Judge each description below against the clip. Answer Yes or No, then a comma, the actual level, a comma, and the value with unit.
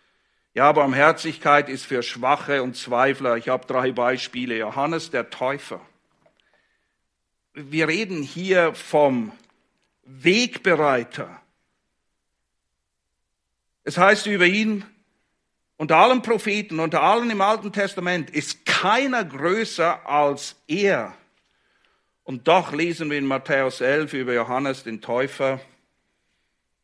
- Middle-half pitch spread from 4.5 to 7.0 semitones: Yes, wide, 5.5 semitones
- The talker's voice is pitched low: No, medium, 145 Hz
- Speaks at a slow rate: Yes, slow, 105 wpm